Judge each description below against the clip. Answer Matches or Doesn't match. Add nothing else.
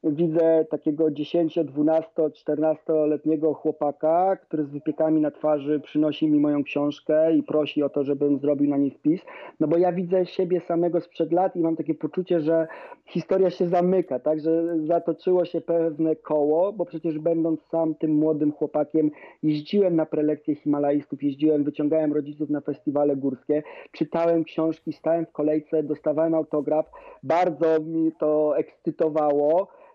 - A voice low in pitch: Doesn't match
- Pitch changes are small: Matches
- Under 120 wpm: Doesn't match